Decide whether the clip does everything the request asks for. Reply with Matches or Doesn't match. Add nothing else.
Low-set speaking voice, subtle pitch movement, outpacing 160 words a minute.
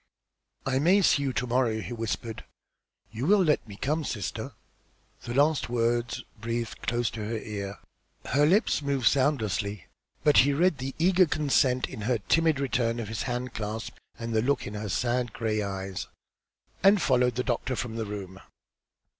Doesn't match